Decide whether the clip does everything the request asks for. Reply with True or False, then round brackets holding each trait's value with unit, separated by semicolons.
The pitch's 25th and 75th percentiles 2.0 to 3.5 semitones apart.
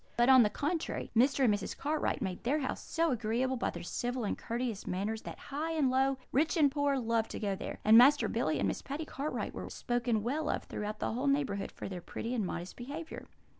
False (4.5 semitones)